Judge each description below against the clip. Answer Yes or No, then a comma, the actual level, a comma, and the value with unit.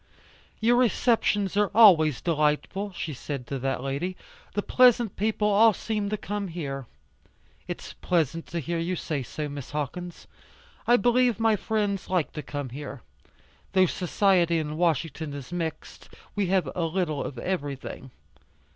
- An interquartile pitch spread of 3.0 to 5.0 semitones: No, wide, 5.6 semitones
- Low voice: No, medium, 175 Hz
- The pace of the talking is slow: No, average, 150 wpm